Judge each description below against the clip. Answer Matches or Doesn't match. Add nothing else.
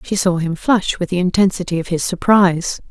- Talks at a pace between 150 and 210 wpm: Matches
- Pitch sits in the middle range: Matches